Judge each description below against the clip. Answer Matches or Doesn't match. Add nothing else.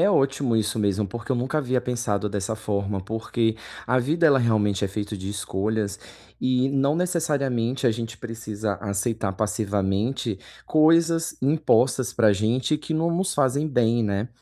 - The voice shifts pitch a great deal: Doesn't match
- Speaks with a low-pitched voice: Matches